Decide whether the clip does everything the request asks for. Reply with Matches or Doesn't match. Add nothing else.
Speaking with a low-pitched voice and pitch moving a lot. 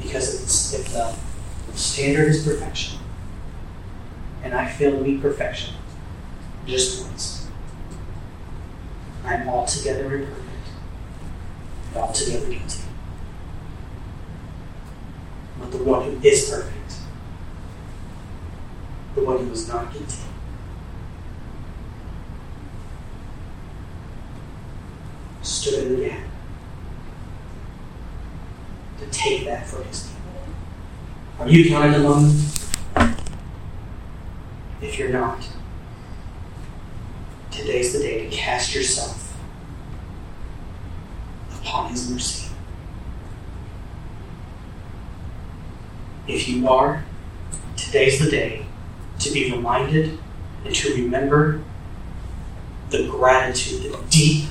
Matches